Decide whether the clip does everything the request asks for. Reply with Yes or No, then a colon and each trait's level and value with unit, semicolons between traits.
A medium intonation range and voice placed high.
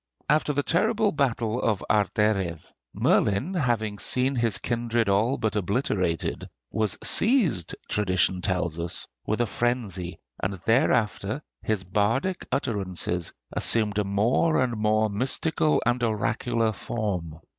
No: average, 4.1 semitones; low, 110 Hz